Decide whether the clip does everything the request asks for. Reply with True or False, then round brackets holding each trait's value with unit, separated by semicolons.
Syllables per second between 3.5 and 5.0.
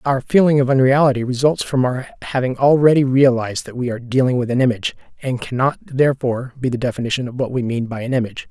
False (6.7 syllables/s)